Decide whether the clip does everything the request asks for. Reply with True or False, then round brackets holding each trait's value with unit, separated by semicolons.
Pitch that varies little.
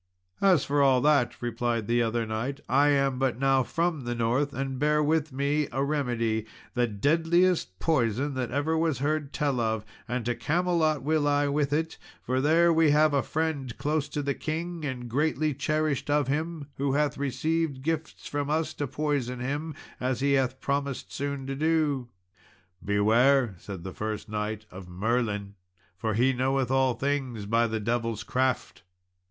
False (3.8 semitones)